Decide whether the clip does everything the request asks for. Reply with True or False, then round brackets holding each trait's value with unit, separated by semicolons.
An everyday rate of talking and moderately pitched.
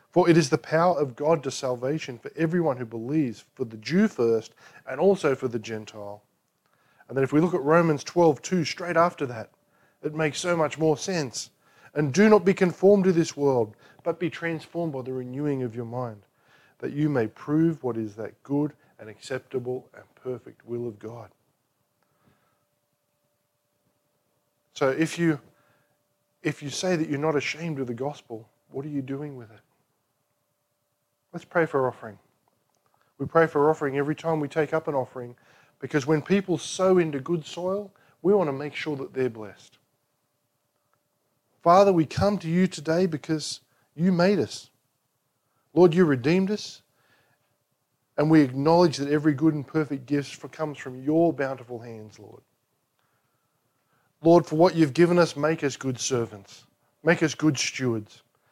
True (170 wpm; 145 Hz)